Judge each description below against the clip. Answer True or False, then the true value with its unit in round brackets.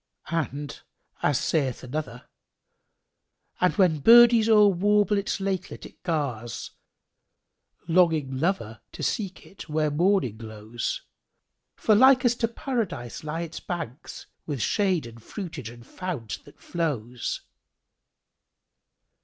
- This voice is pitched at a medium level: True (165 Hz)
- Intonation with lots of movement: True (7.5 semitones)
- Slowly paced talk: True (120 wpm)